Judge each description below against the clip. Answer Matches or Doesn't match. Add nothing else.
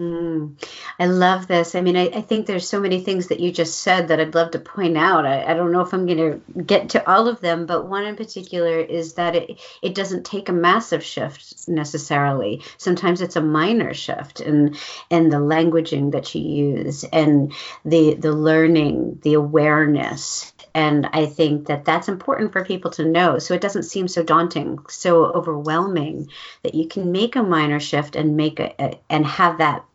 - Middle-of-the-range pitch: Matches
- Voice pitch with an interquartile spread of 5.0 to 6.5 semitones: Doesn't match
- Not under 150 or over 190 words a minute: Doesn't match